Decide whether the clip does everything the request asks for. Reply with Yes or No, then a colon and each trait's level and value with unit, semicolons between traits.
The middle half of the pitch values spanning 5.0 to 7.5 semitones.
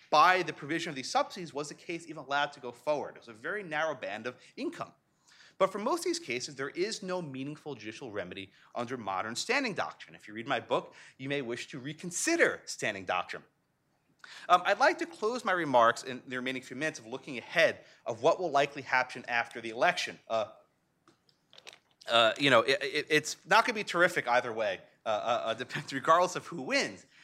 Yes: wide, 5.5 semitones